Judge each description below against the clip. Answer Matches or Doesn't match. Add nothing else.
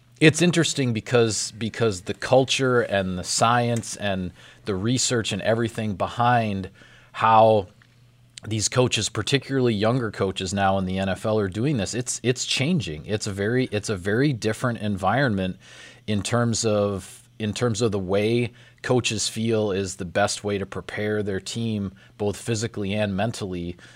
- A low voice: Matches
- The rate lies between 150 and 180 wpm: Matches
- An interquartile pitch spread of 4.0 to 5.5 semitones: Doesn't match